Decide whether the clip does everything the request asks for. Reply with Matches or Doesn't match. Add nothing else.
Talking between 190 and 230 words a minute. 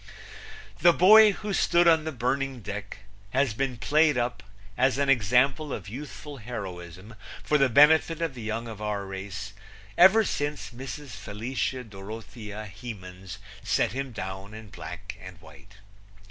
Doesn't match